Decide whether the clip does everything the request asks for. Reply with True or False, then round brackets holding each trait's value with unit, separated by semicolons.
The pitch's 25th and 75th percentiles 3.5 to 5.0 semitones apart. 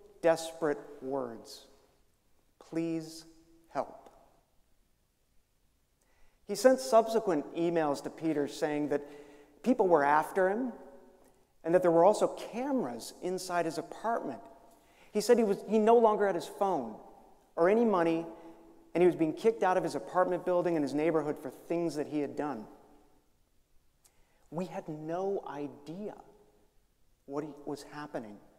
True (4.2 semitones)